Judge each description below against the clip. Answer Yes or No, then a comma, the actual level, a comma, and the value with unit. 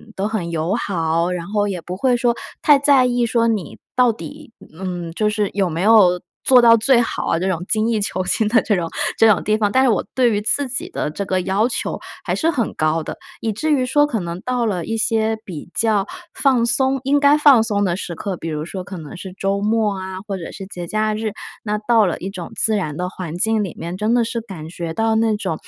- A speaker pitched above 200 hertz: Yes, high, 210 Hz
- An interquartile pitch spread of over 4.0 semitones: Yes, average, 4.4 semitones